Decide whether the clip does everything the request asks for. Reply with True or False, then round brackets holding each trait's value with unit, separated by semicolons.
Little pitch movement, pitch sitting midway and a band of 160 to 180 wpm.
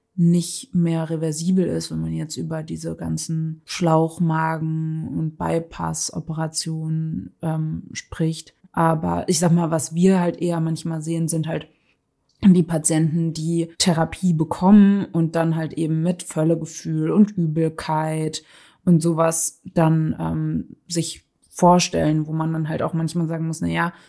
False (1.0 semitones; 160 Hz; 135 wpm)